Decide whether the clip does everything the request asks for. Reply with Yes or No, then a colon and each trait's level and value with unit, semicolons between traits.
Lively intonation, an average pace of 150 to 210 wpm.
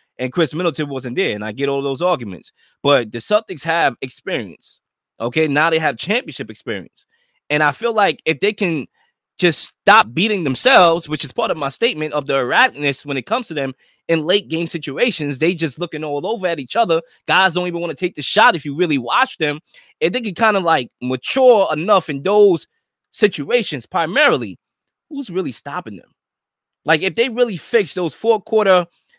Yes: wide, 6.0 semitones; average, 195 wpm